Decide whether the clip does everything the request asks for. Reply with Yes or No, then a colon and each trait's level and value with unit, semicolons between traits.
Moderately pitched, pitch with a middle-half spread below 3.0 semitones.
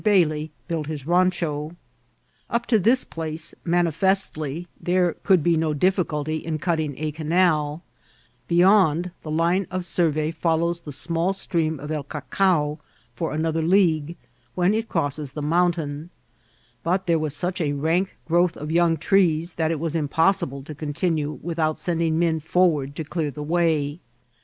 Yes: medium, 165 Hz; narrow, 2.5 semitones